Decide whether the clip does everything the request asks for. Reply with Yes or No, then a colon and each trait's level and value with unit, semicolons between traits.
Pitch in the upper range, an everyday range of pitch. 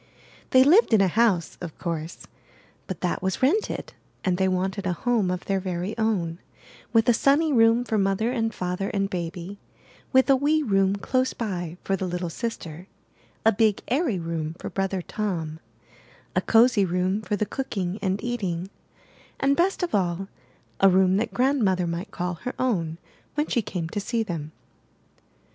Yes: high, 195 Hz; average, 4.5 semitones